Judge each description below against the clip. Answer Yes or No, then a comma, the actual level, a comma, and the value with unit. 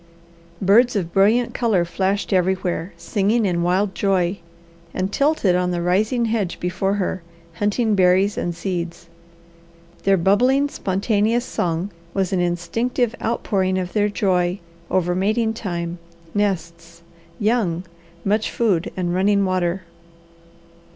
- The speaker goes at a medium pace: No, slow, 125 wpm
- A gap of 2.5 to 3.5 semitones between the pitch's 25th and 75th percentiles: Yes, average, 2.9 semitones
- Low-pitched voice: No, high, 190 Hz